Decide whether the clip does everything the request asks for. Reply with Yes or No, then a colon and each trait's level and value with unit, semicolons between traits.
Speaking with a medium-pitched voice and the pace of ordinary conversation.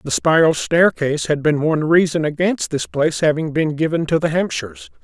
Yes: medium, 160 Hz; average, 190 wpm